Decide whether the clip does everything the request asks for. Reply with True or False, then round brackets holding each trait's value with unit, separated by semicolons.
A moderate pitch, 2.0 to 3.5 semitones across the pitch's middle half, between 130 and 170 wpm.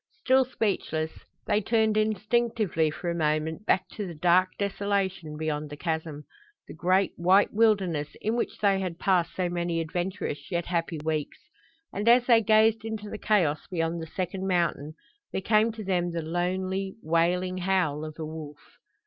False (180 Hz; 4.1 semitones; 165 wpm)